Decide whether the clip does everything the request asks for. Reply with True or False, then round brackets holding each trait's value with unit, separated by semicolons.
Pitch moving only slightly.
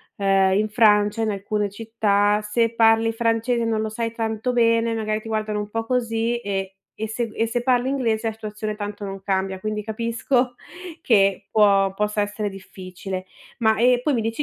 True (1.9 semitones)